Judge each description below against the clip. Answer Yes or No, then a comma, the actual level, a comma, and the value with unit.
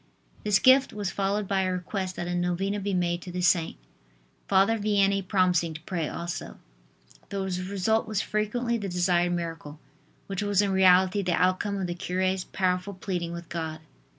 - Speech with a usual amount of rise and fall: No, narrow, 2.3 semitones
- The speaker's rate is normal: Yes, average, 175 wpm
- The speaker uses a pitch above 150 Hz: Yes, medium, 185 Hz